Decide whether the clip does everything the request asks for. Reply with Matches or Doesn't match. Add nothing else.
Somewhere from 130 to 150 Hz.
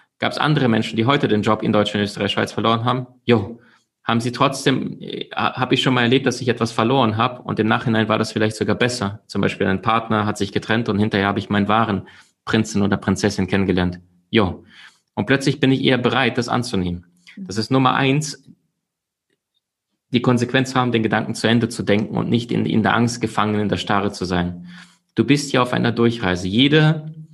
Doesn't match